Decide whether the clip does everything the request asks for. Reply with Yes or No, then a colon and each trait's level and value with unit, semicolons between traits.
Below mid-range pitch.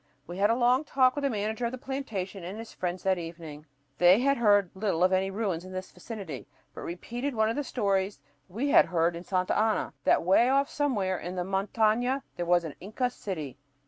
No: high, 200 Hz